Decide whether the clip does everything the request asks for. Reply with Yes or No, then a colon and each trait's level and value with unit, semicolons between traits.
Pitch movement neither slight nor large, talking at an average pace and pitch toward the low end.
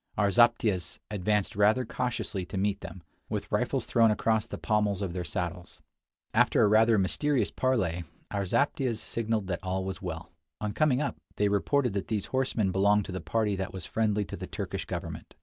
Yes: average, 3.1 semitones; average, 185 wpm; low, 105 Hz